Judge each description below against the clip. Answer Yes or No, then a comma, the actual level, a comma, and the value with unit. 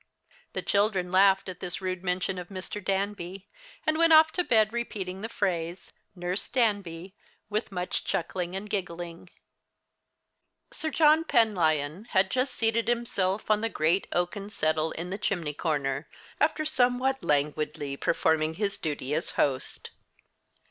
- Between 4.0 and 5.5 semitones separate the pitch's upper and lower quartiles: Yes, average, 4.4 semitones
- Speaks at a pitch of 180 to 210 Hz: Yes, high, 190 Hz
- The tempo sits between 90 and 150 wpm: Yes, average, 140 wpm